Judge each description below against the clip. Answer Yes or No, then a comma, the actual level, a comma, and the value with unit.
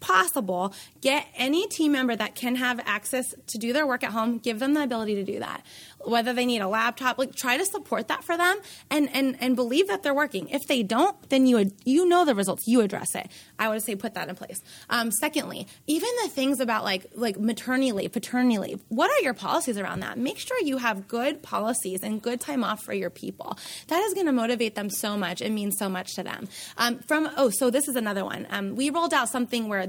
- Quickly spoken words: Yes, fast, 235 wpm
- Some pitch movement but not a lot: Yes, average, 4.6 semitones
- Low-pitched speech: No, high, 245 Hz